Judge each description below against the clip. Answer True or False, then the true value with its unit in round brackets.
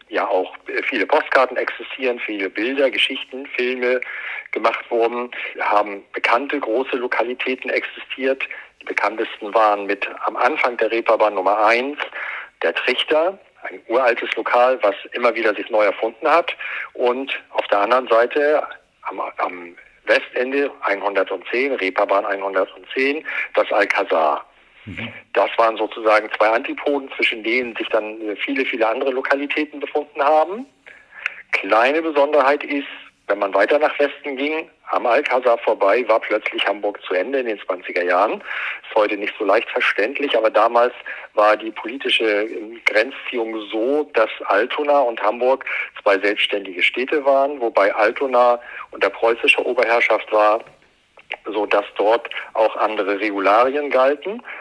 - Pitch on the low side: True (125 Hz)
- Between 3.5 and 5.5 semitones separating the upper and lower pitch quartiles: True (4.8 semitones)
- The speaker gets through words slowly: False (135 wpm)